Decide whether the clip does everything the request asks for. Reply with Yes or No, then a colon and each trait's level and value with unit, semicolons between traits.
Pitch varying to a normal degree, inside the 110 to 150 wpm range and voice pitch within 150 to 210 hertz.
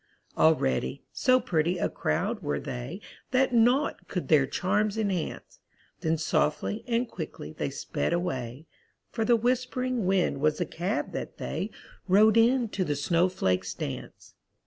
No: wide, 7.1 semitones; average, 145 wpm; medium, 185 Hz